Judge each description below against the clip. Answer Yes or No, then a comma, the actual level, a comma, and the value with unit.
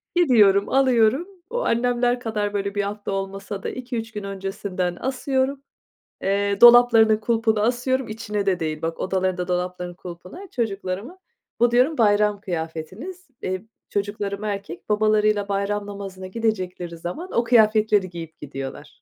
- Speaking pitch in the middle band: No, high, 205 Hz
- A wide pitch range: No, average, 3.8 semitones